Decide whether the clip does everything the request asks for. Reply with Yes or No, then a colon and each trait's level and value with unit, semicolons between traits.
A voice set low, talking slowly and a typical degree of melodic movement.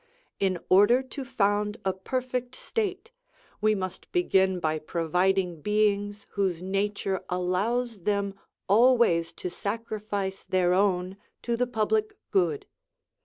No: high, 200 Hz; slow, 120 wpm; average, 4.1 semitones